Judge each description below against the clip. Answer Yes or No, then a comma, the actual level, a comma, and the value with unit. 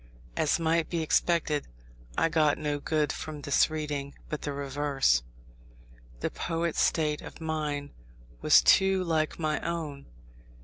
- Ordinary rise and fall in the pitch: No, narrow, 2.1 semitones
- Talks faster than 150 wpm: No, slow, 135 wpm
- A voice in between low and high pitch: Yes, medium, 155 Hz